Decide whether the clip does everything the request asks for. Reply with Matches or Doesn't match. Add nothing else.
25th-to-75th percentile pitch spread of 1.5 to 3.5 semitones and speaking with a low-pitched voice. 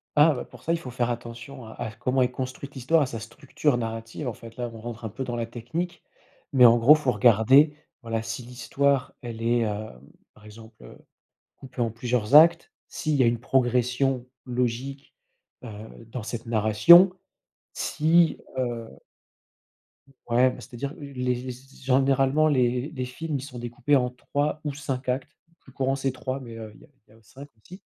Matches